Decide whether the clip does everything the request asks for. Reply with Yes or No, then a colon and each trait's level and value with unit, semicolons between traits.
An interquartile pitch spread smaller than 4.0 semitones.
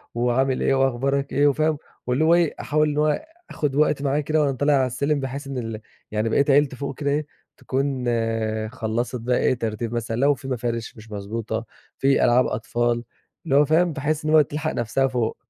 Yes: average, 3.4 semitones